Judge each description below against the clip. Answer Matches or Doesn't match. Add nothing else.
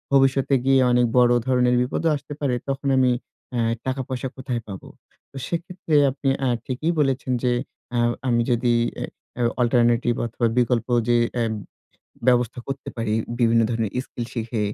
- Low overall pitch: Matches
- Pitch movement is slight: Matches